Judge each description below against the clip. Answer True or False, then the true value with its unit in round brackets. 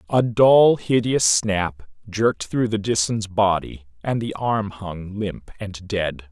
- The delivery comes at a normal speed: True (150 wpm)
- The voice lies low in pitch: True (100 Hz)